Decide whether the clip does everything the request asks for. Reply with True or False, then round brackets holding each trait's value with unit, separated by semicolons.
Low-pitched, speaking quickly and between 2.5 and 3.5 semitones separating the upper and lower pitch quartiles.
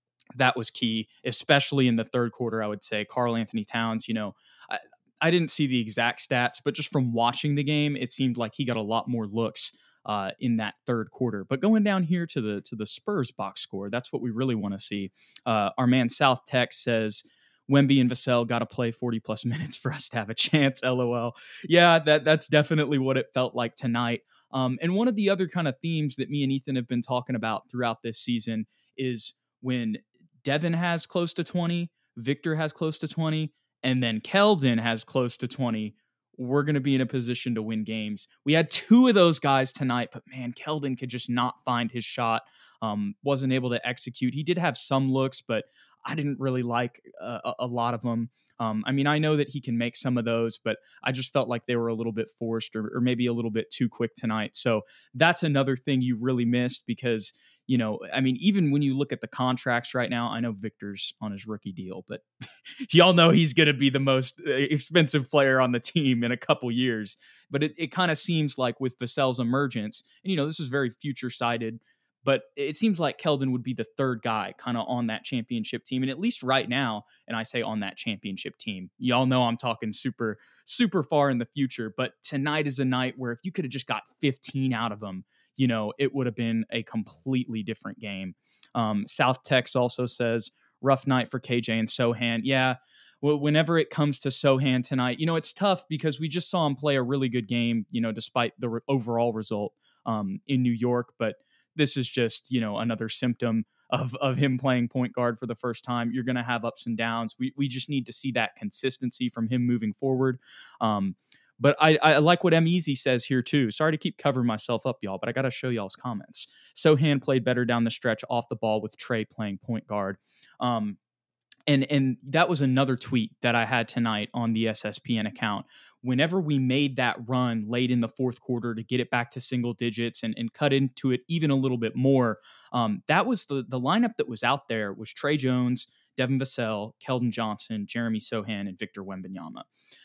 True (125 Hz; 220 wpm; 3.2 semitones)